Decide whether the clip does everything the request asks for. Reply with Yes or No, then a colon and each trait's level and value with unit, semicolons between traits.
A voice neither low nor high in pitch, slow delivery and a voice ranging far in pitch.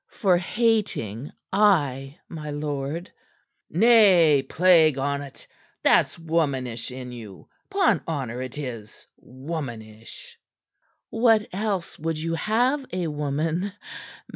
Yes: medium, 155 Hz; slow, 100 wpm; wide, 6.1 semitones